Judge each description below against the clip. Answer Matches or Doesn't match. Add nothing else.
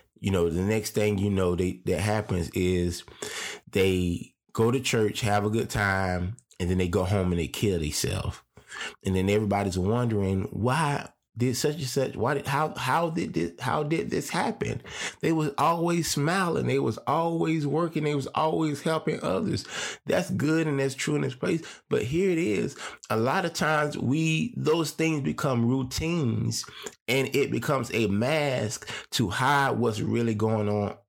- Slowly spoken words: Doesn't match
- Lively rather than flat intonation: Matches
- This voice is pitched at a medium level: Doesn't match